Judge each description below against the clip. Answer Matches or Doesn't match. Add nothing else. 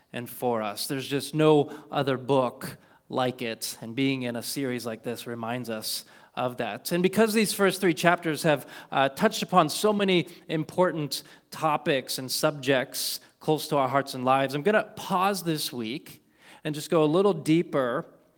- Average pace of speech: Matches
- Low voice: Doesn't match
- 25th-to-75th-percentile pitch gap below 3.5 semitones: Doesn't match